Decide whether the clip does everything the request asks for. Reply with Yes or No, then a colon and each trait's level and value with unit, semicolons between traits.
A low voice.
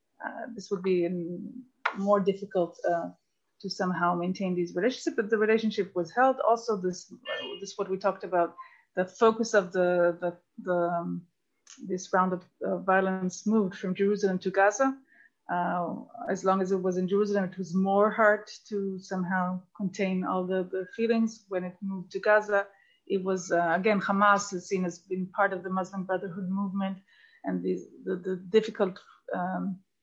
No: high, 190 Hz